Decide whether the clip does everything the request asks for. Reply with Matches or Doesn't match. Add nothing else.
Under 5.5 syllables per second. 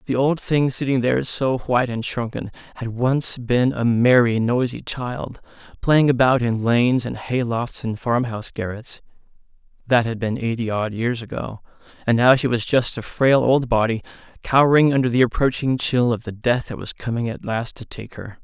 Matches